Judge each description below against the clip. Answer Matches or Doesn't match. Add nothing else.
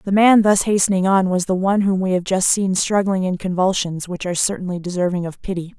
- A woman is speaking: Matches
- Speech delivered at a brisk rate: Matches